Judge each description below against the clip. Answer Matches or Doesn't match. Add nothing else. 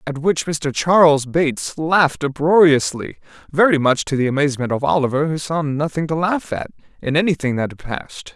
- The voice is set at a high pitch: Doesn't match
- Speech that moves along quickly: Doesn't match